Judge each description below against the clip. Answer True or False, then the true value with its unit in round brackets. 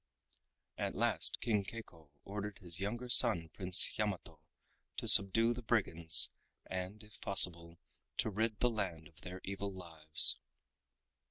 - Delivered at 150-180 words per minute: False (135 wpm)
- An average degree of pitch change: True (3.9 semitones)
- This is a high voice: False (100 Hz)